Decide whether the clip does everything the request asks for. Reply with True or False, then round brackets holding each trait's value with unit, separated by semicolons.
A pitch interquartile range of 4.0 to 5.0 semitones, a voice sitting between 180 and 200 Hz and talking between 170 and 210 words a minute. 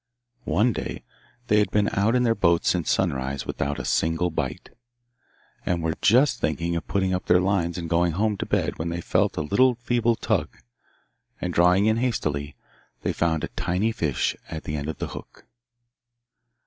False (4.6 semitones; 90 Hz; 185 wpm)